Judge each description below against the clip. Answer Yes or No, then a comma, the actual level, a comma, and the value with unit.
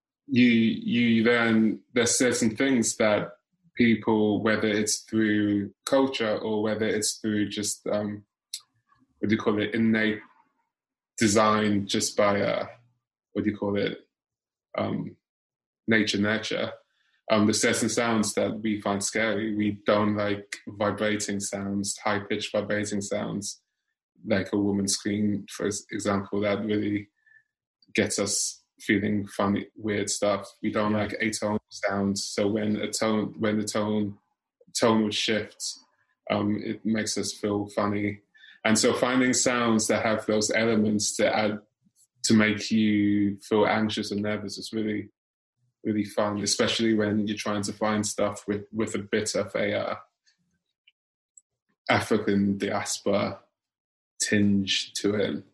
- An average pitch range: No, narrow, 1.2 semitones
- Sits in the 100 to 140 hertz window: Yes, low, 105 Hz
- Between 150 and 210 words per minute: No, slow, 135 wpm